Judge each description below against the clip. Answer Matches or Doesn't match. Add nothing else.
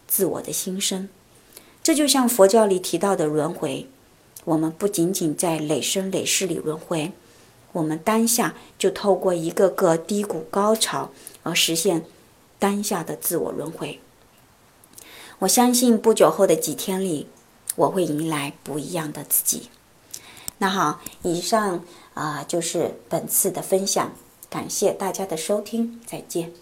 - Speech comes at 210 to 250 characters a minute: Matches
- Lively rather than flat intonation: Doesn't match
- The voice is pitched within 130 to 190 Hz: Matches